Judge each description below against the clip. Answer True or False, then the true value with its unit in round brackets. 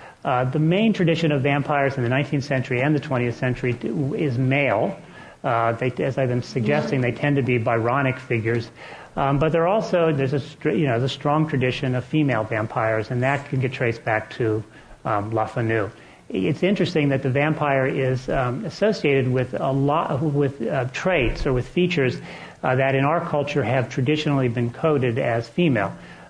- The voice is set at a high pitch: False (135 Hz)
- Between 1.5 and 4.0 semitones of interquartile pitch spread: True (3.1 semitones)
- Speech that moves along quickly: False (190 wpm)